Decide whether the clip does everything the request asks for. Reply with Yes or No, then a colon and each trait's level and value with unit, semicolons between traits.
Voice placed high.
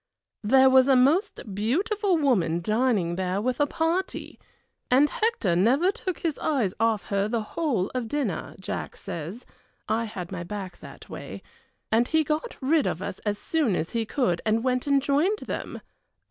Yes: high, 245 Hz